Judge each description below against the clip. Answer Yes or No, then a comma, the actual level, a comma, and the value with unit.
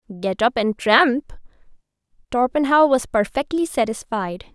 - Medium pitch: No, high, 245 Hz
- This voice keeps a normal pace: No, slow, 105 wpm